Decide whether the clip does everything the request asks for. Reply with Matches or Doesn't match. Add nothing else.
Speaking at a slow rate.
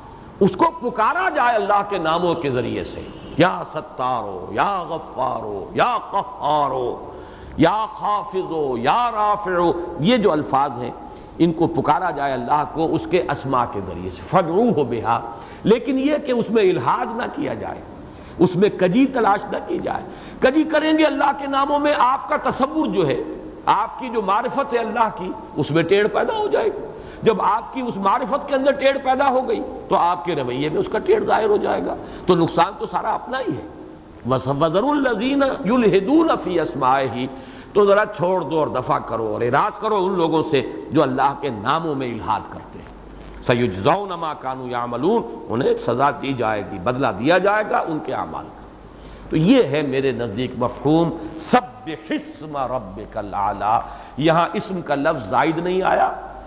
Doesn't match